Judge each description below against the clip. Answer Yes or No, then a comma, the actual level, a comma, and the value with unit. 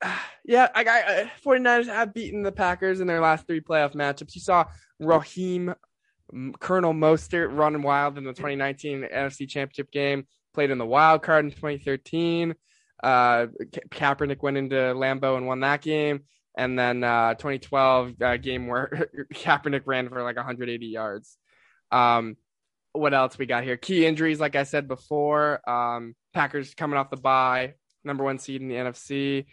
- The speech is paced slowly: No, average, 165 wpm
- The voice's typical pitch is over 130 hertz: Yes, medium, 140 Hz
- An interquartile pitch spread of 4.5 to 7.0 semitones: No, average, 3.3 semitones